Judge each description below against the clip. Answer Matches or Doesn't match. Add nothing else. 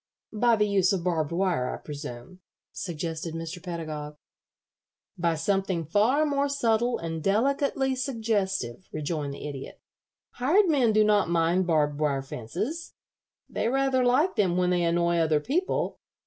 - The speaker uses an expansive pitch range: Matches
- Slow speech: Doesn't match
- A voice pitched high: Doesn't match